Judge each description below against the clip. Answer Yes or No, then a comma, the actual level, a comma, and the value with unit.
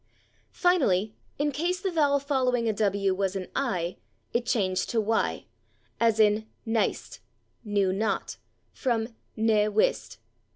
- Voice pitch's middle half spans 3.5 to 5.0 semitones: Yes, average, 4.5 semitones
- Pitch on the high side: Yes, high, 220 Hz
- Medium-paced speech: No, slow, 130 wpm